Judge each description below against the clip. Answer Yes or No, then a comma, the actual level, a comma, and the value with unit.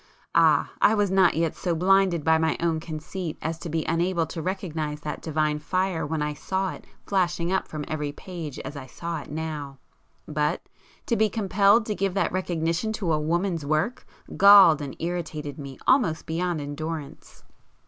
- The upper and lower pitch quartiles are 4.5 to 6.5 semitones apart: No, average, 3.5 semitones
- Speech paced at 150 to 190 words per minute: Yes, average, 180 wpm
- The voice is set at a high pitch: No, medium, 165 Hz